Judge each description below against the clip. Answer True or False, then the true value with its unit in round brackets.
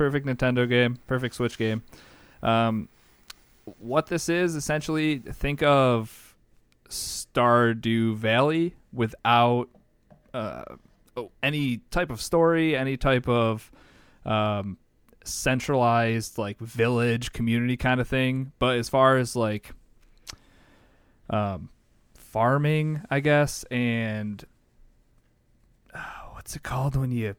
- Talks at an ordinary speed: False (105 wpm)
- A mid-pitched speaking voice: False (120 Hz)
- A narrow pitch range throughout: False (3.4 semitones)